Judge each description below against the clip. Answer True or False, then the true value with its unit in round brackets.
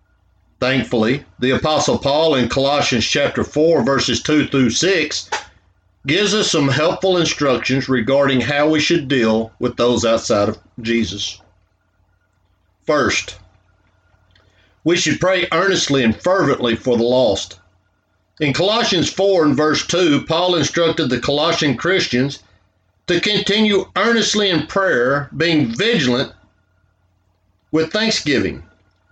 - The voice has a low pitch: True (125 Hz)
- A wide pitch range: True (8.7 semitones)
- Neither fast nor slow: False (115 wpm)